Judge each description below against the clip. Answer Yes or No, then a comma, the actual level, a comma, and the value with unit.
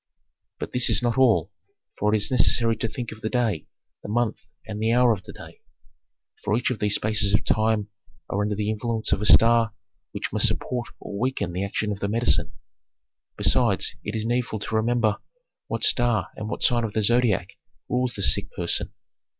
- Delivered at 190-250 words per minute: Yes, average, 200 wpm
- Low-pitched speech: Yes, low, 110 Hz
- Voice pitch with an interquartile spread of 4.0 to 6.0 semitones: No, narrow, 2.4 semitones